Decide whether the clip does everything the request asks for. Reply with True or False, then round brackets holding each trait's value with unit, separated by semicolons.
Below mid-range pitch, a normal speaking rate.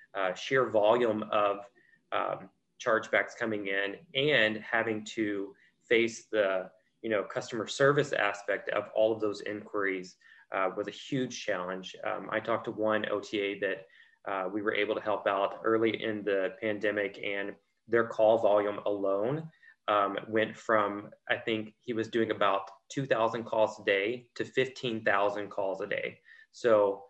True (110 Hz; 160 wpm)